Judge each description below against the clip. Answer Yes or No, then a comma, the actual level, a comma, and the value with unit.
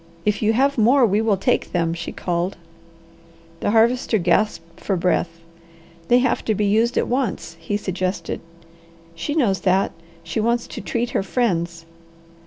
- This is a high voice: Yes, high, 205 Hz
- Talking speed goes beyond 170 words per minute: No, average, 160 wpm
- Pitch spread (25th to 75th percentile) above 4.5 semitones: Yes, average, 4.9 semitones